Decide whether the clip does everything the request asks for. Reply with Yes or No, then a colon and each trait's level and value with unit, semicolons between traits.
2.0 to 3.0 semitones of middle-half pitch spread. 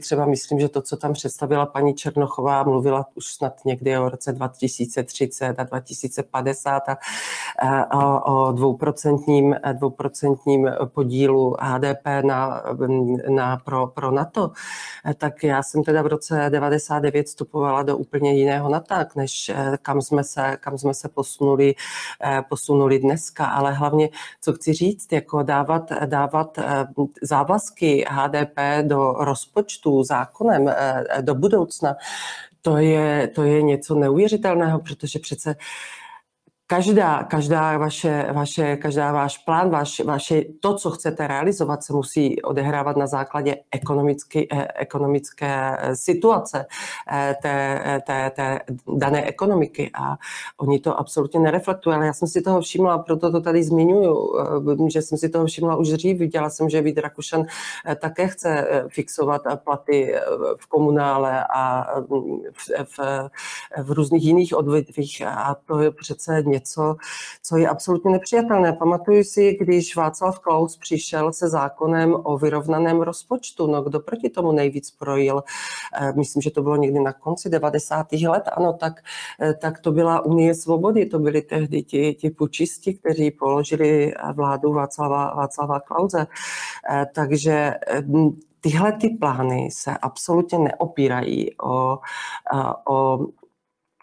Yes: narrow, 2.5 semitones